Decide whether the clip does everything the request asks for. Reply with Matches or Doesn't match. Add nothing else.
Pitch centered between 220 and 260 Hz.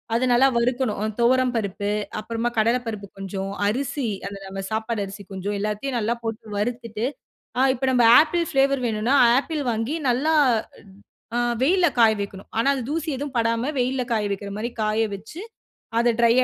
Matches